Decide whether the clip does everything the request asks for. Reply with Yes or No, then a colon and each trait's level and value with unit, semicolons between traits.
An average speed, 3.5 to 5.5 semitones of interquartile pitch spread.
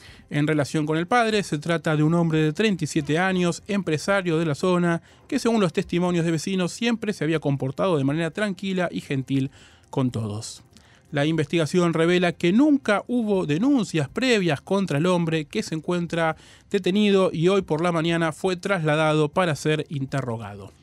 Yes: average, 170 wpm; average, 4.0 semitones